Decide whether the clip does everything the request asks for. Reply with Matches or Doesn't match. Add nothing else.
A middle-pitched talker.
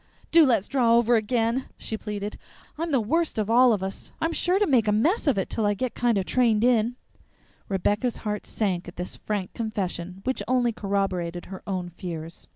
Doesn't match